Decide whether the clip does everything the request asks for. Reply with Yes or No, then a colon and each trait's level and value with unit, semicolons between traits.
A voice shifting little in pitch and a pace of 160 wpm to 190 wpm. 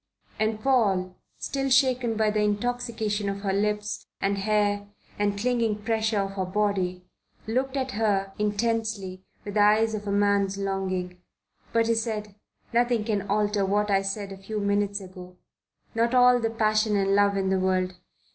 Yes: narrow, 2.2 semitones; average, 165 wpm